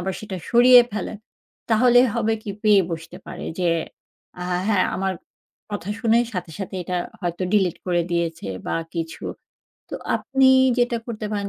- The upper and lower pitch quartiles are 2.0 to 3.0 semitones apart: No, average, 4.3 semitones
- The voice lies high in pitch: Yes, high, 200 Hz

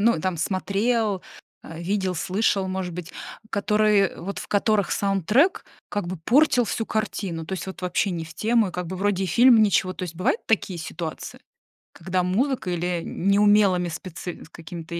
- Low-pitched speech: No, high, 190 Hz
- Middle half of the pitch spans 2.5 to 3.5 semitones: Yes, average, 3.0 semitones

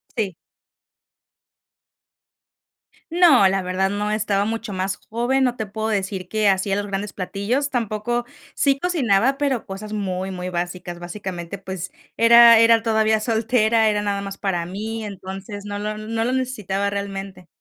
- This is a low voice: No, high, 205 Hz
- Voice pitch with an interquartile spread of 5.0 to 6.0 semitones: No, average, 2.9 semitones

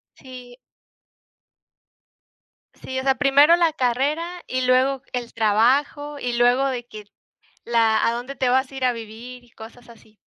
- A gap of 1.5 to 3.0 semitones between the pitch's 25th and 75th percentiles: Yes, narrow, 2.4 semitones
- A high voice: Yes, very high, 250 Hz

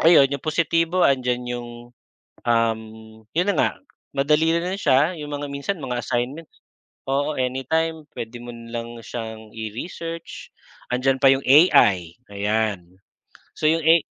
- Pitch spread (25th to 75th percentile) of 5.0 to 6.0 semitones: Yes, wide, 5.4 semitones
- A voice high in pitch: No, low, 135 Hz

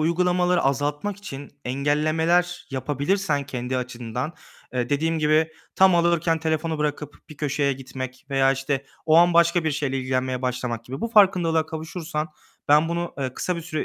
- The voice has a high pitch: No, medium, 150 Hz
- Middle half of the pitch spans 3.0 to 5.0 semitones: Yes, average, 4.0 semitones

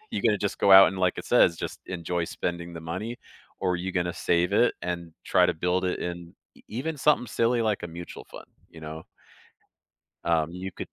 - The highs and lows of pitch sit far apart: No, narrow, 2.6 semitones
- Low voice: Yes, very low, 90 Hz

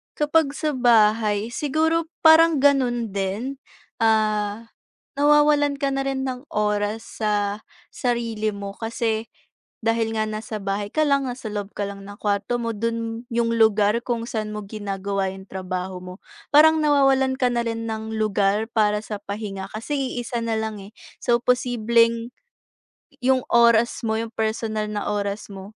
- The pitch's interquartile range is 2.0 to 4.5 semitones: Yes, average, 2.9 semitones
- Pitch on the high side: Yes, high, 225 Hz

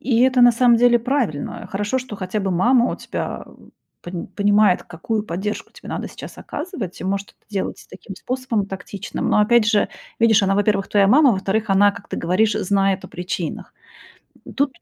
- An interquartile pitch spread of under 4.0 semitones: Yes, average, 3.6 semitones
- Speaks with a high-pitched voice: Yes, high, 210 Hz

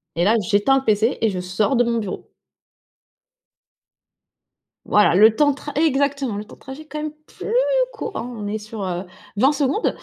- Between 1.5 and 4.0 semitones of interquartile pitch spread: No, wide, 5.4 semitones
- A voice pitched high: Yes, high, 230 Hz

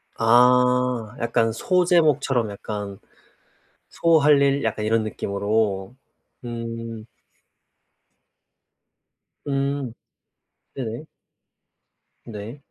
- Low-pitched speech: Yes, low, 115 Hz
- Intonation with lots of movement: No, average, 3.9 semitones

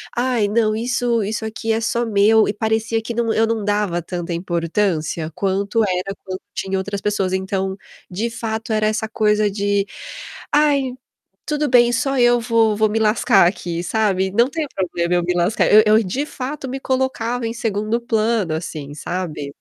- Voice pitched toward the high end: Yes, high, 215 Hz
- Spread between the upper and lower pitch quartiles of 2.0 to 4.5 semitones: Yes, average, 3.5 semitones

